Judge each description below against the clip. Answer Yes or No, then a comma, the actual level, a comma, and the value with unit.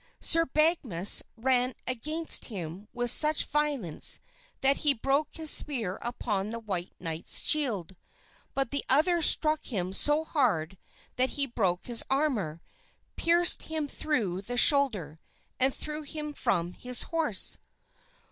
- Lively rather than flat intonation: Yes, wide, 7.4 semitones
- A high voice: Yes, very high, 255 Hz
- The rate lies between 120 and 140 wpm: Yes, slow, 135 wpm